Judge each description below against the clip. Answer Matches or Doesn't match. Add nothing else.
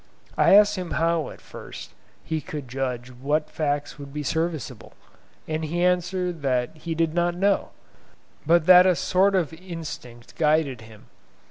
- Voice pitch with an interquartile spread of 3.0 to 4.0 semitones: Matches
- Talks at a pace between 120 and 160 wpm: Matches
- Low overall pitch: Doesn't match